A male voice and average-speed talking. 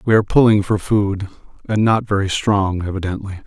Yes: male; average, 175 wpm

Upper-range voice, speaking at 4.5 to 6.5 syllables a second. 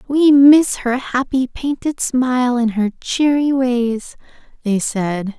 No: very high, 250 Hz; 3.4 syllables/s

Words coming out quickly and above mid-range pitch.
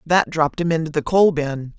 No: fast, 235 wpm; medium, 160 Hz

